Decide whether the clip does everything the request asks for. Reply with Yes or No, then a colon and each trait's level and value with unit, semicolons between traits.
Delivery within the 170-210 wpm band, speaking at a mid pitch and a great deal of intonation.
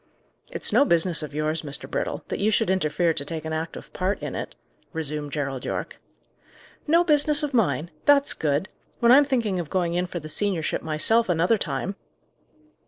Yes: average, 180 wpm; medium, 175 Hz; wide, 6.3 semitones